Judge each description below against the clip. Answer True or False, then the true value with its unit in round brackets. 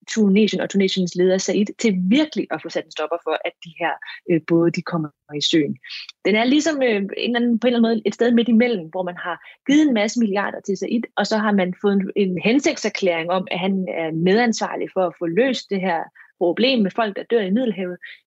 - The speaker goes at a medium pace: False (240 wpm)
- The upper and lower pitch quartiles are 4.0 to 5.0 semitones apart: True (4.3 semitones)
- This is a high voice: True (200 Hz)